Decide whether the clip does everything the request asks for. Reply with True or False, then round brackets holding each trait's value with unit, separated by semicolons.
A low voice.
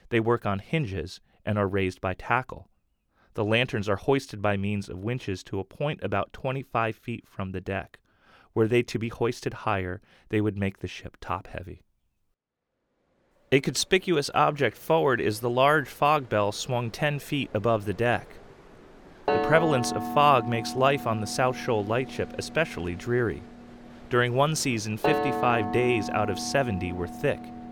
True (115 Hz)